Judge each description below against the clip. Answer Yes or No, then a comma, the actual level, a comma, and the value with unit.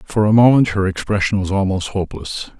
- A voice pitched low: Yes, low, 100 Hz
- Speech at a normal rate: Yes, average, 185 wpm